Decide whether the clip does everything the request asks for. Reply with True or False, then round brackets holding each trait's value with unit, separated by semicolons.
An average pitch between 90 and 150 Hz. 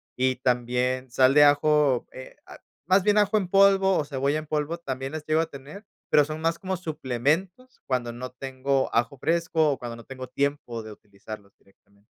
True (140 Hz)